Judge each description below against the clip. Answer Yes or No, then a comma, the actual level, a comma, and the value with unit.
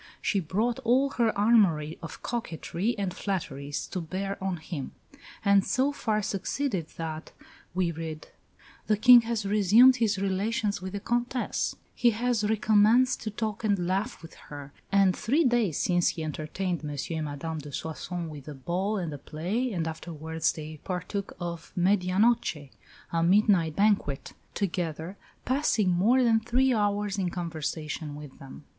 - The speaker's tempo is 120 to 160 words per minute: Yes, average, 155 wpm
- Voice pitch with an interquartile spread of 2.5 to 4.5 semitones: No, average, 5.2 semitones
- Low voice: No, high, 190 Hz